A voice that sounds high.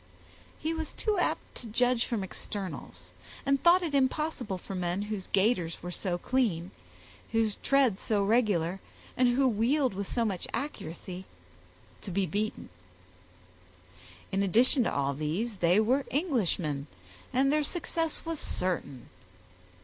Yes: high, 215 Hz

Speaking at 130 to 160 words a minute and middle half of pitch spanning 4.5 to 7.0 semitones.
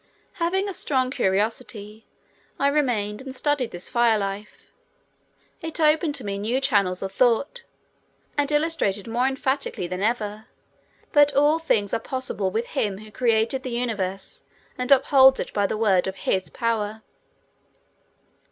Yes: average, 145 wpm; average, 5.1 semitones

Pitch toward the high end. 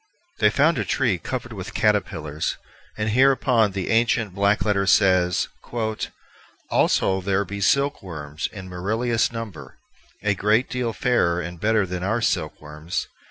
No: low, 100 Hz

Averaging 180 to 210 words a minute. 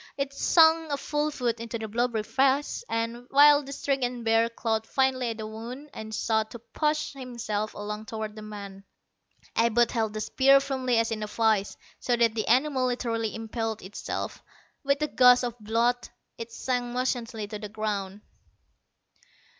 No: average, 170 wpm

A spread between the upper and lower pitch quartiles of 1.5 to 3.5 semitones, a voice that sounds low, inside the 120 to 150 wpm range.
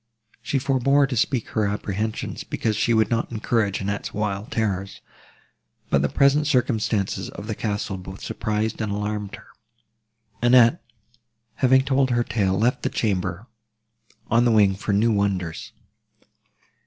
Yes: average, 3.1 semitones; low, 110 Hz; average, 140 wpm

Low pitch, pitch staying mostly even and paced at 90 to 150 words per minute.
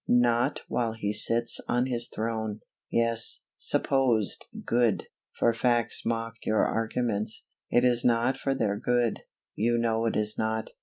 Yes: low, 115 Hz; narrow, 1.5 semitones; average, 145 wpm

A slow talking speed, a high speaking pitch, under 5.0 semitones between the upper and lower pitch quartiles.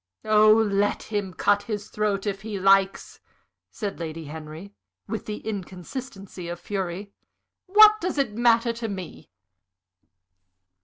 Yes: slow, 125 wpm; high, 205 Hz; narrow, 2.6 semitones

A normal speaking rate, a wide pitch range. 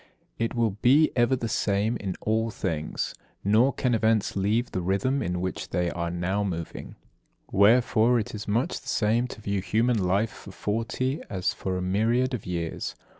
No: average, 175 wpm; average, 3.9 semitones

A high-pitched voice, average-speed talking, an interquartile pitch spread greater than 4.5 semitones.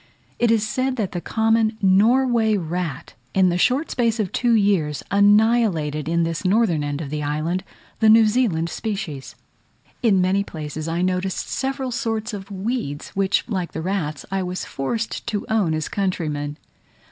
Yes: high, 195 Hz; average, 165 wpm; average, 5.3 semitones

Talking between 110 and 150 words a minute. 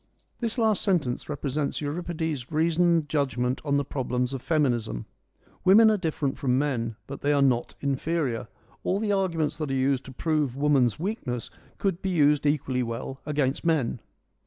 No: average, 160 wpm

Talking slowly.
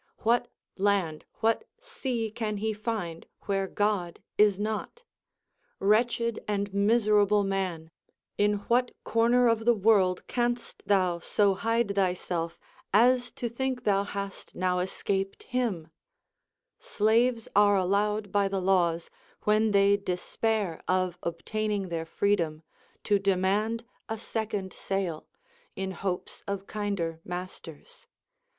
Yes: slow, 125 wpm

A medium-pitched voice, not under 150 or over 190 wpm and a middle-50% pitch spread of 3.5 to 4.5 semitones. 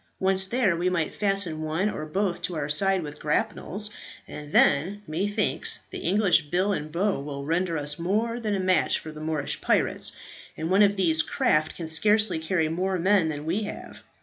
Yes: medium, 175 Hz; average, 185 wpm; average, 4.1 semitones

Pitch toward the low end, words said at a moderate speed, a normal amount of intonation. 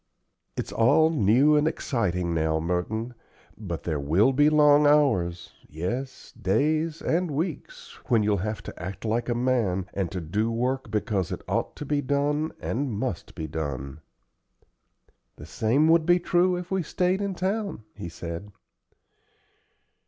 No: low, 120 Hz; average, 150 wpm; wide, 8.7 semitones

